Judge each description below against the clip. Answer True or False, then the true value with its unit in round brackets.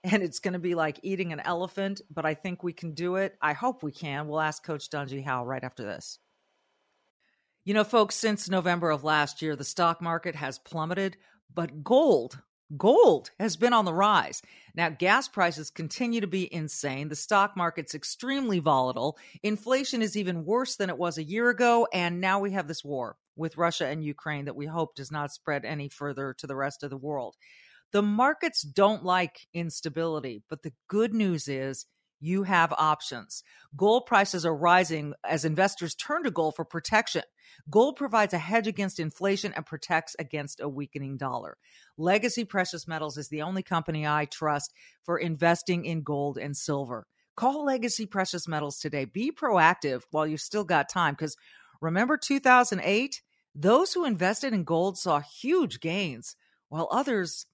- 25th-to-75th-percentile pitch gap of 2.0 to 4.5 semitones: False (5.1 semitones)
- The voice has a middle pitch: True (170 Hz)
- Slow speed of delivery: False (175 wpm)